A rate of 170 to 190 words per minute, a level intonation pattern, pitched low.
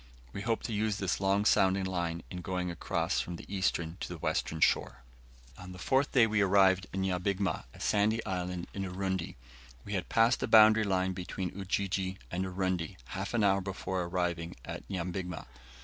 Yes: average, 180 wpm; narrow, 1.8 semitones; very low, 95 Hz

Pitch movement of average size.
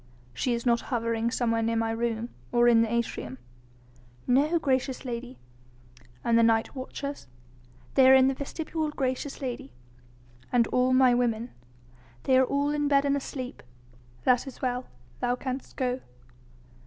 No: narrow, 2.3 semitones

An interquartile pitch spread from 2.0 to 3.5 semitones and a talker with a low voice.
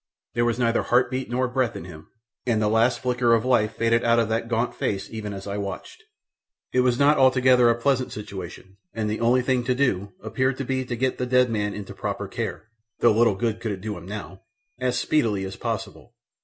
Yes: average, 3.1 semitones; low, 115 Hz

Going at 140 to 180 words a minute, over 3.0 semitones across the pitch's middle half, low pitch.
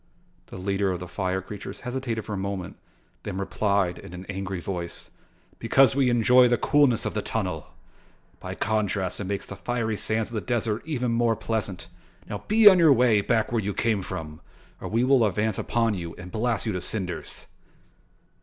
No: average, 190 wpm; average, 3.8 semitones; low, 105 Hz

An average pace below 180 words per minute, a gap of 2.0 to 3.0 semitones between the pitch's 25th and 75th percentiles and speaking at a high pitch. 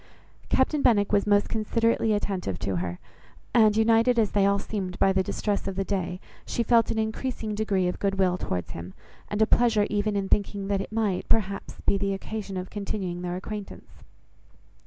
No: average, 190 wpm; narrow, 2.4 semitones; high, 205 Hz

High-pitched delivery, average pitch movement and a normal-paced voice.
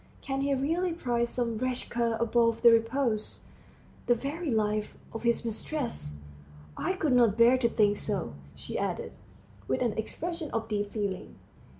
Yes: high, 235 Hz; average, 3.6 semitones; average, 160 wpm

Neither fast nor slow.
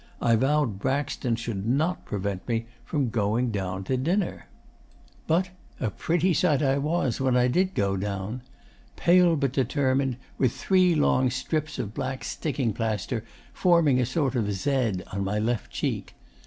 Yes: average, 155 wpm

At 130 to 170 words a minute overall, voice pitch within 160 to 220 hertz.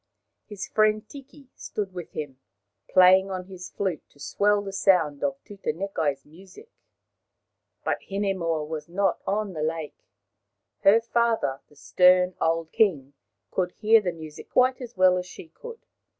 Yes: average, 150 wpm; medium, 185 Hz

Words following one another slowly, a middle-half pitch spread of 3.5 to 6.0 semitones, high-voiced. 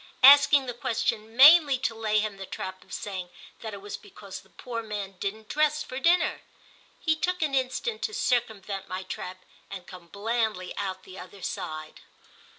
No: average, 175 wpm; wide, 5.6 semitones; high, 215 Hz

